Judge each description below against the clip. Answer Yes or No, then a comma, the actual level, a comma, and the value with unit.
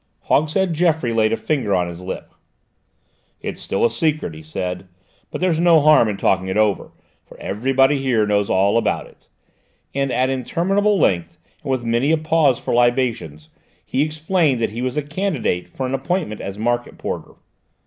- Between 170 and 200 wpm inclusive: Yes, average, 180 wpm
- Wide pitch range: Yes, wide, 6.7 semitones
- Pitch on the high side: No, low, 130 Hz